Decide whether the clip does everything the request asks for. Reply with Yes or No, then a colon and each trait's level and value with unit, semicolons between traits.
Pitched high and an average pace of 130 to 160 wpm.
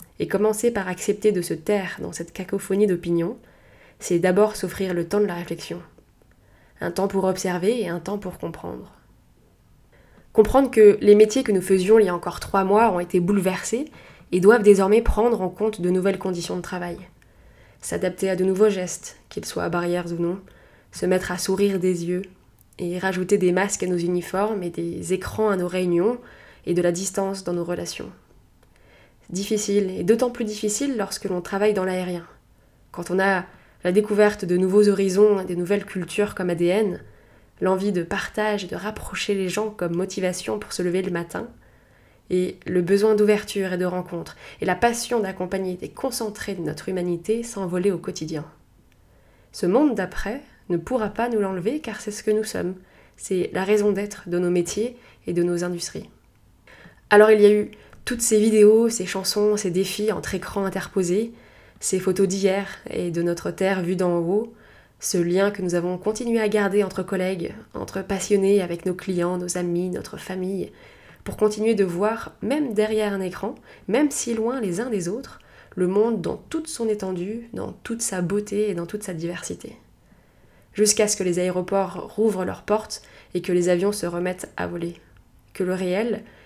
No: high, 195 Hz; average, 185 wpm